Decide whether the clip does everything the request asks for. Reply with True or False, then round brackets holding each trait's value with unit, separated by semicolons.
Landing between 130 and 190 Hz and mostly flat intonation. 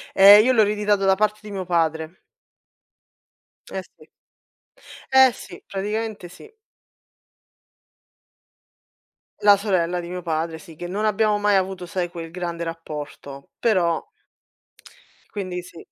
False (185 Hz; 3.6 semitones)